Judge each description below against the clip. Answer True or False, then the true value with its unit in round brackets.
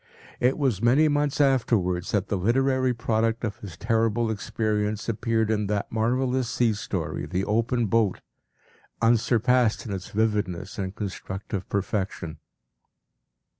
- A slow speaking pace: True (130 wpm)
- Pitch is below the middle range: True (110 Hz)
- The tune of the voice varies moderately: True (3.0 semitones)